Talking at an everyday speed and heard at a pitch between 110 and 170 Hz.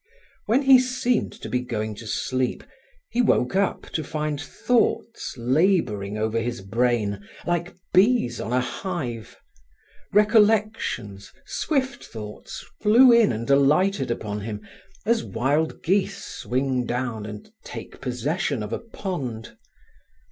No: slow, 125 wpm; low, 135 Hz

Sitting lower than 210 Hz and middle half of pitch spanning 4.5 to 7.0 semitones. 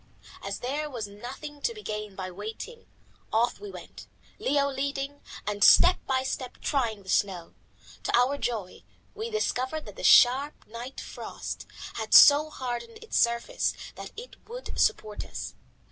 No: very high, 260 Hz; wide, 5.6 semitones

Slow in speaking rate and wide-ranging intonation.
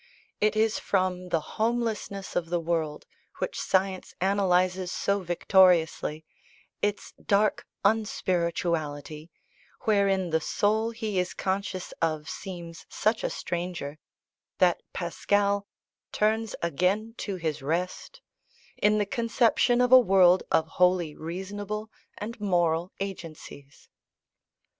No: slow, 110 wpm; average, 3.4 semitones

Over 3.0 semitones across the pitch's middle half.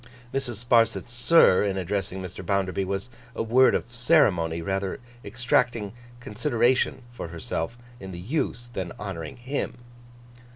Yes: average, 4.3 semitones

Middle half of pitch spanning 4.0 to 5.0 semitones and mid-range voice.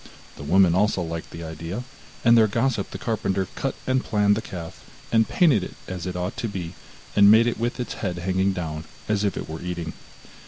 No: average, 4.3 semitones; very low, 95 Hz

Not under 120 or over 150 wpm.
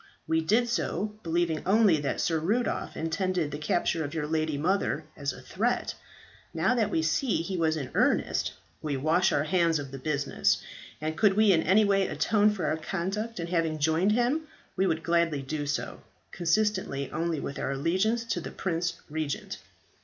No: average, 185 wpm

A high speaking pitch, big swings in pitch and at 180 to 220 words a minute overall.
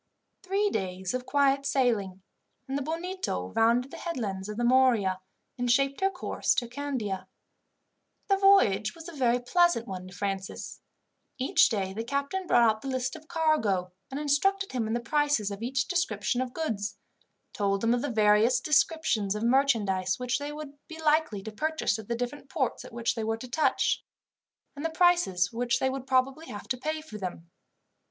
Yes: very high, 250 Hz; wide, 5.8 semitones; average, 185 wpm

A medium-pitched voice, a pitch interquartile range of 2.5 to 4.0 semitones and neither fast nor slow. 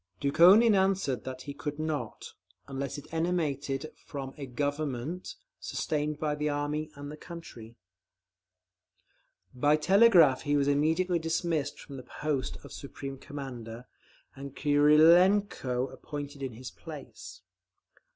No: medium, 145 Hz; average, 2.9 semitones; slow, 120 wpm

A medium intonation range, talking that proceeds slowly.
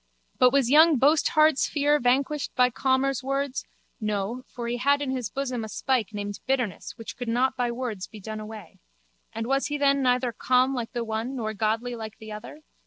No: average, 3.5 semitones; average, 195 wpm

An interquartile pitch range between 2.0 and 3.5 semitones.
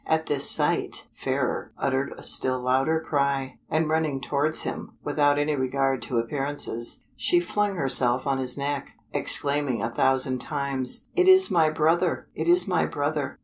Yes: average, 3.0 semitones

